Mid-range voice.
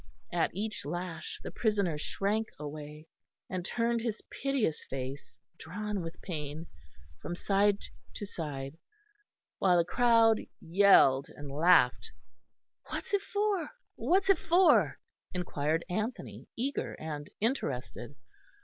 Yes: medium, 180 Hz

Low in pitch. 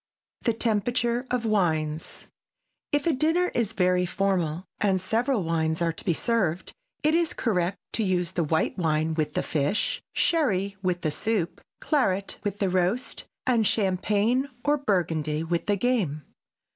No: high, 195 Hz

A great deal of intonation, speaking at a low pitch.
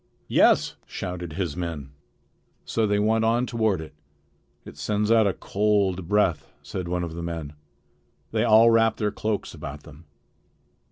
No: average, 4.5 semitones; low, 100 Hz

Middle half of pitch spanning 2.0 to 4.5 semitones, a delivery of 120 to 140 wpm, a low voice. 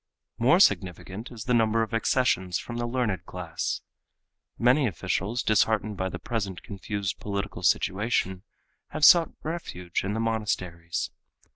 Yes: average, 4.2 semitones; slow, 135 wpm; low, 105 Hz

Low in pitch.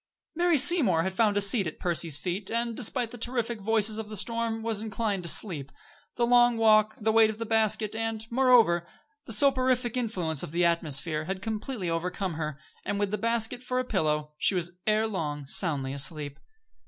No: high, 215 Hz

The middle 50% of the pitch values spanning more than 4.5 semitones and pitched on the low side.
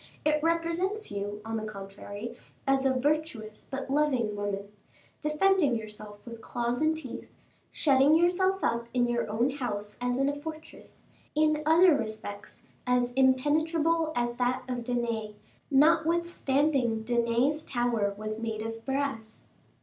No: wide, 5.5 semitones; very high, 250 Hz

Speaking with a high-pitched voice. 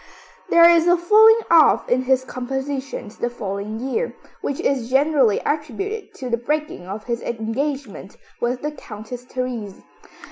Yes: very high, 260 Hz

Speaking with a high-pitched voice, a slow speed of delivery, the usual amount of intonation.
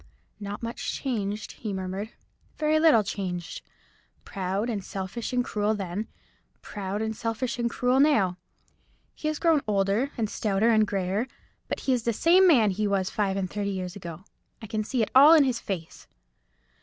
No: high, 215 Hz; average, 170 wpm; average, 3.9 semitones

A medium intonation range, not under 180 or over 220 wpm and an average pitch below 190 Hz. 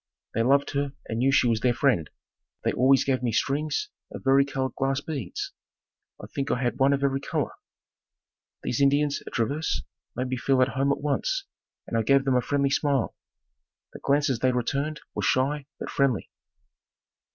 No: narrow, 1.8 semitones; average, 185 wpm; low, 135 Hz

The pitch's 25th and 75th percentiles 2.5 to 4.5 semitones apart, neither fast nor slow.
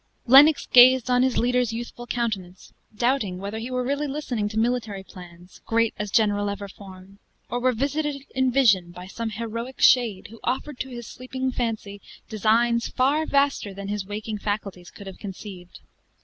Yes: average, 4.0 semitones; average, 170 wpm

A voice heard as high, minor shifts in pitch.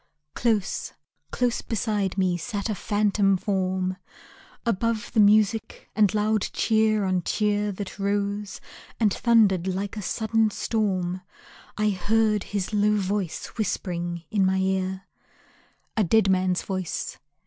Yes: high, 205 Hz; narrow, 2.3 semitones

